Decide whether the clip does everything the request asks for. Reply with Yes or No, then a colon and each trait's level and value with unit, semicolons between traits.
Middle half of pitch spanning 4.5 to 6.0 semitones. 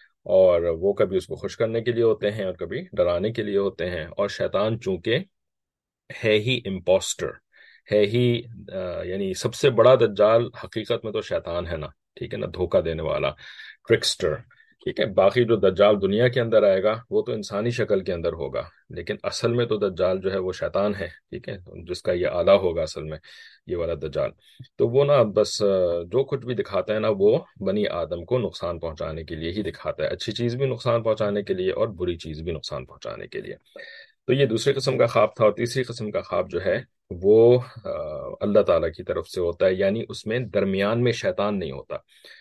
Yes: average, 5.3 semitones